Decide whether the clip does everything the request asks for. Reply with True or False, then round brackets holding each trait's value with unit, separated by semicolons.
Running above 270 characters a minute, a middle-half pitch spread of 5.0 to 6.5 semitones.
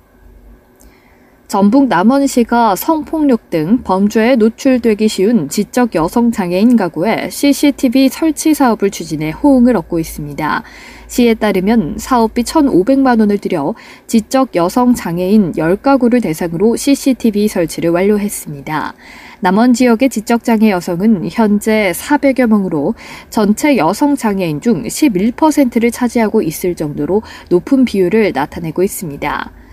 True (280 characters per minute; 5.3 semitones)